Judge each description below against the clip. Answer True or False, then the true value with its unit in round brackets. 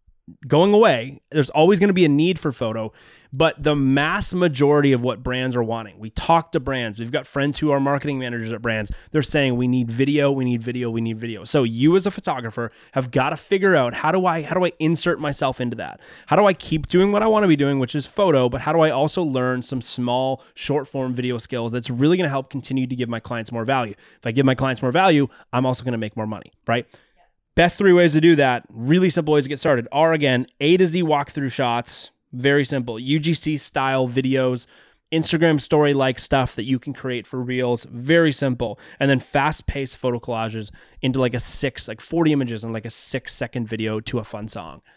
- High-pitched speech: False (135 Hz)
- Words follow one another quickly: True (235 wpm)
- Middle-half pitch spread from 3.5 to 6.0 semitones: True (4.0 semitones)